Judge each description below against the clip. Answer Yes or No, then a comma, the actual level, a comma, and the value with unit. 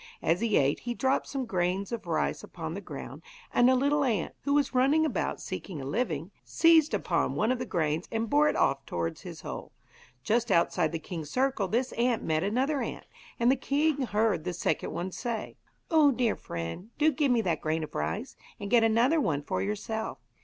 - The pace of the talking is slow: No, fast, 205 wpm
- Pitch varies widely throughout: Yes, wide, 7.7 semitones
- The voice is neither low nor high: No, high, 225 Hz